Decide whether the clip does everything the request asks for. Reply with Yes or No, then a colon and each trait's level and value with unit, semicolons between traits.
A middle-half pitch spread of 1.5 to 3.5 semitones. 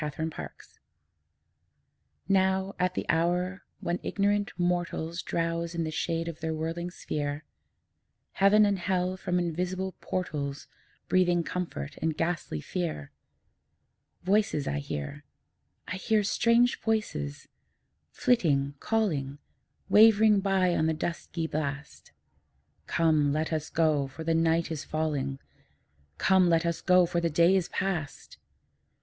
Yes: average, 3.2 semitones